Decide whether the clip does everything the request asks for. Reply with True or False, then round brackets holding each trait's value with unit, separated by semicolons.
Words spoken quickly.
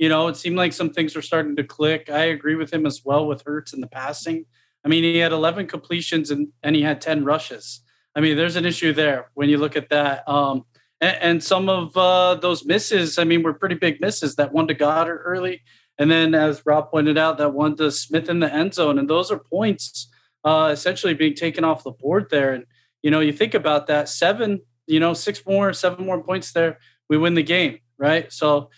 True (235 wpm)